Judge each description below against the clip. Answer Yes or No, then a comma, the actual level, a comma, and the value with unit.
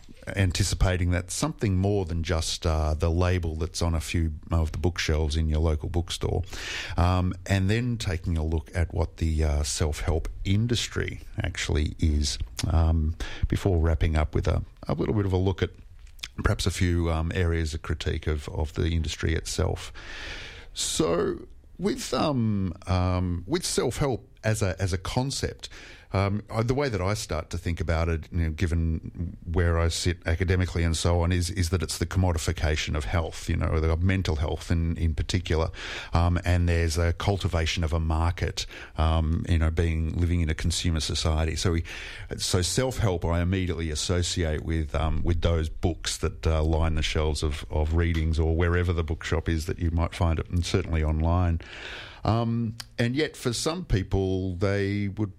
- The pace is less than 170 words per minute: No, average, 180 wpm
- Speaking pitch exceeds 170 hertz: No, very low, 85 Hz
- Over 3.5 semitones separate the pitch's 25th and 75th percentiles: No, average, 2.8 semitones